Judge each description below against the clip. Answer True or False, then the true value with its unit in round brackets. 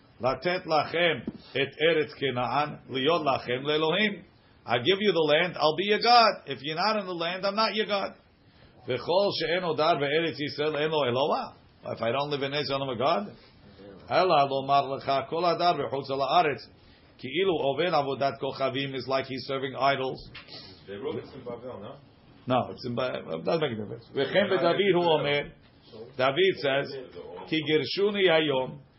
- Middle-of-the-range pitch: True (145 Hz)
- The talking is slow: True (95 wpm)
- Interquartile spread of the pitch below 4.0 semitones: False (4.4 semitones)